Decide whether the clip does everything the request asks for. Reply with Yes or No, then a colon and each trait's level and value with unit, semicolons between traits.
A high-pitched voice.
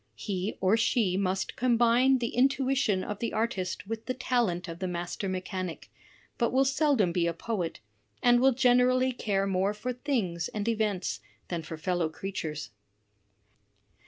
Yes: high, 210 Hz